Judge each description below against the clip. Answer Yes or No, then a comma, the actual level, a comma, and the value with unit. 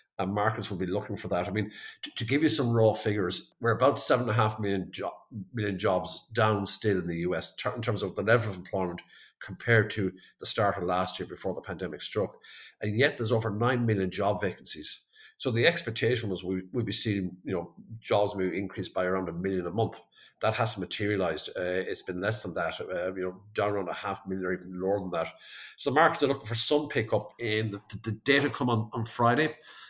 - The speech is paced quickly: Yes, fast, 225 wpm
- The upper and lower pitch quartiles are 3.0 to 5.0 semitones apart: Yes, average, 3.8 semitones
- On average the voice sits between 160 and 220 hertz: No, low, 105 Hz